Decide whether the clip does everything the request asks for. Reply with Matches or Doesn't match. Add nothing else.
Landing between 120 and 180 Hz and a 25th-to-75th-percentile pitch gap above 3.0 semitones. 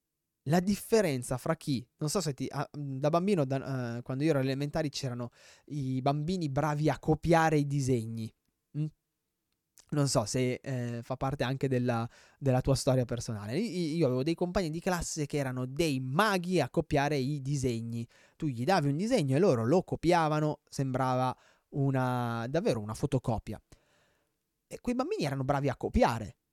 Matches